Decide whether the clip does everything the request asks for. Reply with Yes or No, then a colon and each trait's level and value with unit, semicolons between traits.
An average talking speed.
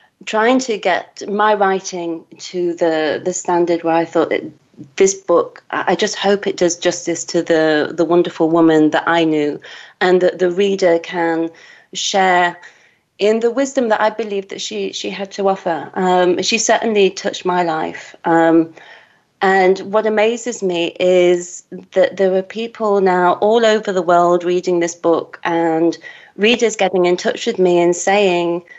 Yes: average, 165 wpm